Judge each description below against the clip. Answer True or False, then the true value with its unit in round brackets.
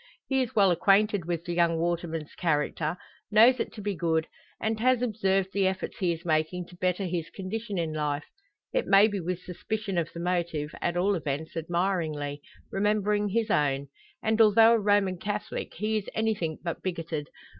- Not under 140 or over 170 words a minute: False (180 wpm)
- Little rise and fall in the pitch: False (4.1 semitones)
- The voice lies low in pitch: False (185 Hz)